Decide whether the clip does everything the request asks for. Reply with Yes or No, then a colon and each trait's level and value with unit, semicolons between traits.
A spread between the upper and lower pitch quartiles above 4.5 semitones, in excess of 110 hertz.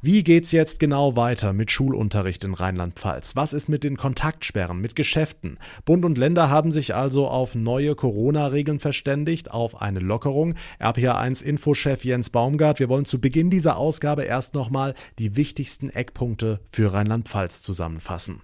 Yes: average, 5.1 semitones; low, 135 Hz